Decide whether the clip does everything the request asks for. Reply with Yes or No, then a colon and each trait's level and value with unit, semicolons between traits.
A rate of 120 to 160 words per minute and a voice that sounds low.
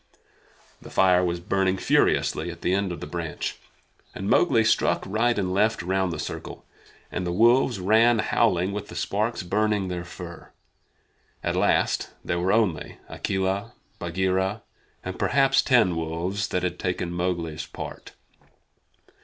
Yes: average, 145 wpm; very low, 95 Hz